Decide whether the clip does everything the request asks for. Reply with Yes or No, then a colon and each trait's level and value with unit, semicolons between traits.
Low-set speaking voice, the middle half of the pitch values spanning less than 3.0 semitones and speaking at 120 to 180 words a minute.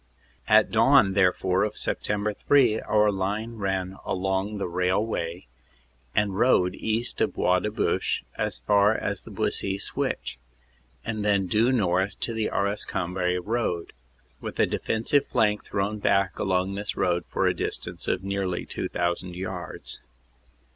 Yes: low, 100 Hz; narrow, 2.6 semitones; average, 145 wpm